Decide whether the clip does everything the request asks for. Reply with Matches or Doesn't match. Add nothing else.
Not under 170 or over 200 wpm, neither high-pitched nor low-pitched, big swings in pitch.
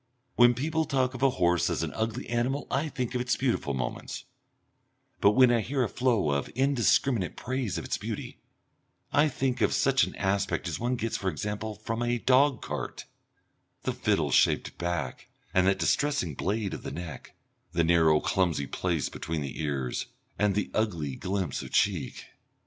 Doesn't match